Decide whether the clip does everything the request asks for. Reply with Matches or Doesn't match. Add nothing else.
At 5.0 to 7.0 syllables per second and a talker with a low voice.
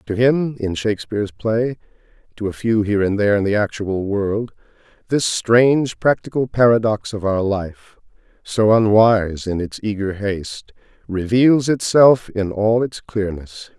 Doesn't match